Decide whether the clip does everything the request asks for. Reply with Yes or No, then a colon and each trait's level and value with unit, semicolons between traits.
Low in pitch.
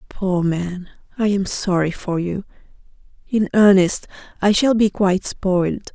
No: high, 190 Hz